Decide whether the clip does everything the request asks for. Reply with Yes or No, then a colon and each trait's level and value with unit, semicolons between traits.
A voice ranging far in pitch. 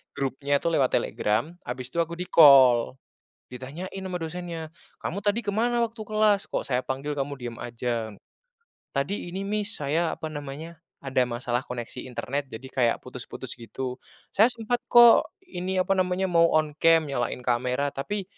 Yes: wide, 6.3 semitones